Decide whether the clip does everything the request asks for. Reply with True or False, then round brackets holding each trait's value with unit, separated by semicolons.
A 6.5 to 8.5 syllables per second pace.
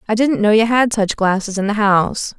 False (5.5 syllables/s)